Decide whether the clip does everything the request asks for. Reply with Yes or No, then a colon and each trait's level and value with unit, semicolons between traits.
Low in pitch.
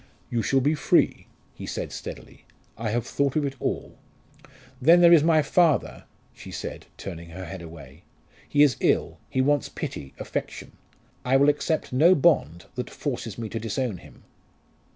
Yes: low, 130 Hz